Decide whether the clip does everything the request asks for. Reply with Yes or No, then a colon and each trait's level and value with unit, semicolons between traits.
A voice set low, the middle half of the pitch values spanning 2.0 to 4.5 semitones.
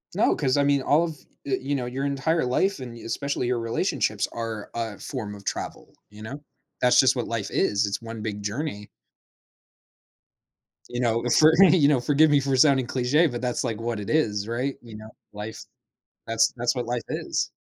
Yes: low, 125 Hz; average, 3.7 semitones